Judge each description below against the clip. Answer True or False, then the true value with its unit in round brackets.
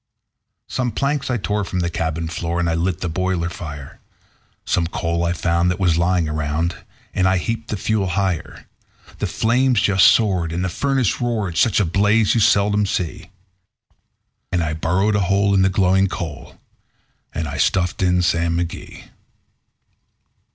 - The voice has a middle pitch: False (90 Hz)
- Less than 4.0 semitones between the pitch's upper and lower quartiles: True (3.4 semitones)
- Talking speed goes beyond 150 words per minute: True (165 wpm)